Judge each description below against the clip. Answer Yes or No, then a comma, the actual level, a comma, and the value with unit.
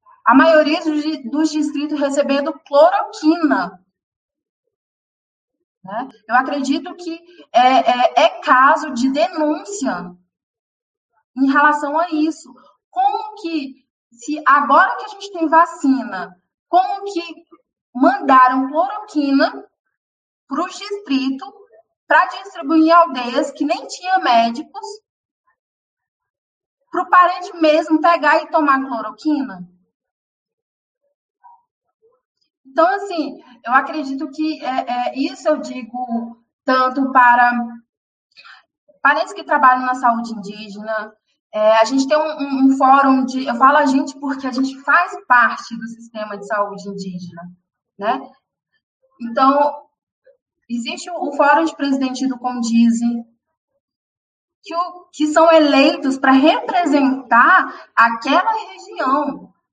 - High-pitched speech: Yes, very high, 290 Hz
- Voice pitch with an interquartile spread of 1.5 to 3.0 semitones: No, average, 4.9 semitones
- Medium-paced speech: No, slow, 110 wpm